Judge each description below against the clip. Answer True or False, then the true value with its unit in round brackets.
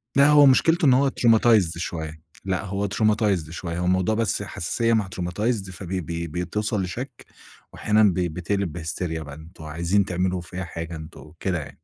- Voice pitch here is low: True (95 Hz)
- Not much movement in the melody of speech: False (4.1 semitones)